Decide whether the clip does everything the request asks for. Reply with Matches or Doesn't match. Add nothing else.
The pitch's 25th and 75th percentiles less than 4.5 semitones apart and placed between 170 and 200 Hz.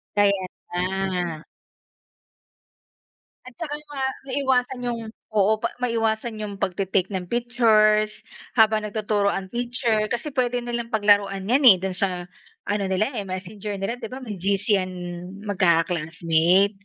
Doesn't match